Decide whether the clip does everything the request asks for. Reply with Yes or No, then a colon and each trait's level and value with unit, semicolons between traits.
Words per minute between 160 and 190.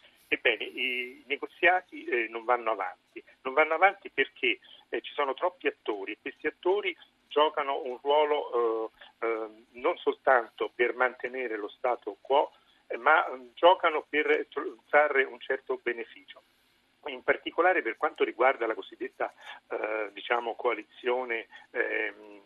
No: slow, 115 wpm